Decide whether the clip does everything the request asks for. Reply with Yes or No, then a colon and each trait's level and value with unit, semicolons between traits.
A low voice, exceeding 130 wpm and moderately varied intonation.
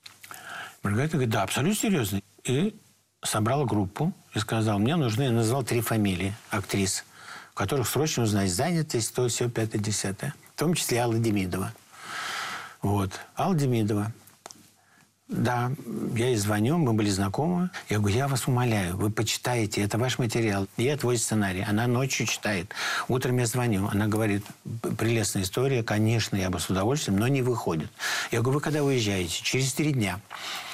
Yes: low, 115 Hz; average, 155 wpm; average, 4.2 semitones